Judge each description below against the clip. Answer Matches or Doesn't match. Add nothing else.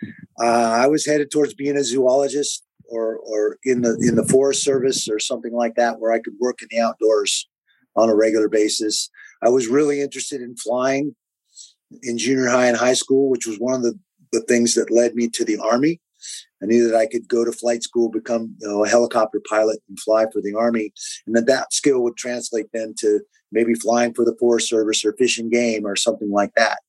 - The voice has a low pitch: Matches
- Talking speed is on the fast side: Matches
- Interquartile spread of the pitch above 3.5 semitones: Doesn't match